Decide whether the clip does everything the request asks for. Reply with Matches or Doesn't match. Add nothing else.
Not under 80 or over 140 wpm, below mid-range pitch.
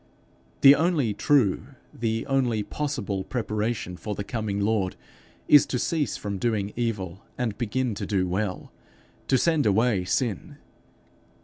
Matches